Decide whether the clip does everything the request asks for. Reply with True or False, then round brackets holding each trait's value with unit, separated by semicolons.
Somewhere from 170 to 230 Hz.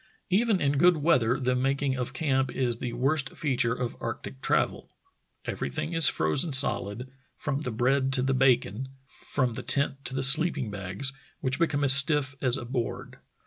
False (135 Hz)